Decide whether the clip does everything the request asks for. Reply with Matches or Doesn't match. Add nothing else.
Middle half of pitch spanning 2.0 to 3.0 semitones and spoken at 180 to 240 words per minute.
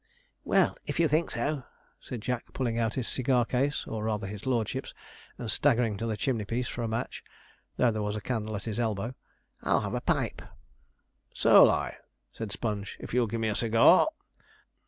Matches